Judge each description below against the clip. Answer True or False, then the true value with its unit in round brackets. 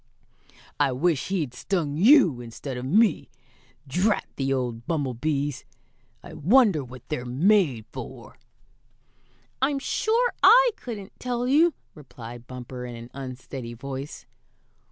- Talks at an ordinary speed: False (120 wpm)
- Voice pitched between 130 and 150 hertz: True (140 Hz)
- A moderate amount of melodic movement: False (8.3 semitones)